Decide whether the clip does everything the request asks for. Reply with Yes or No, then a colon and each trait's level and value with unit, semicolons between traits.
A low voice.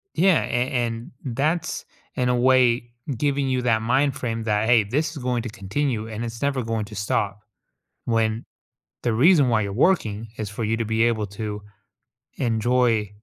Yes: low, 115 Hz